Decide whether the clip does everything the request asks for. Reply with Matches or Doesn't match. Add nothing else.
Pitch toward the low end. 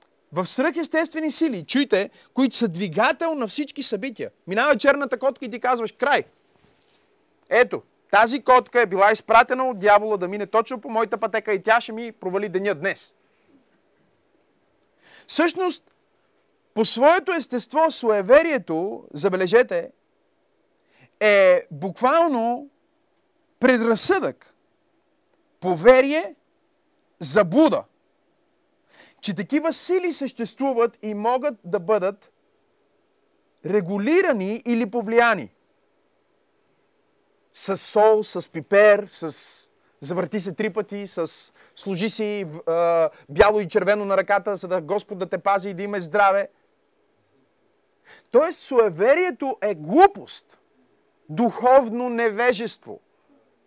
Doesn't match